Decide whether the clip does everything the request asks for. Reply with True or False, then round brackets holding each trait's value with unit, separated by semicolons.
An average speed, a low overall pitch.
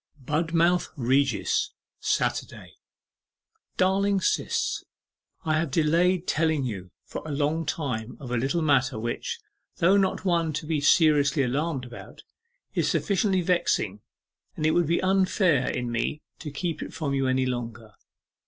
False (145 wpm; 150 Hz)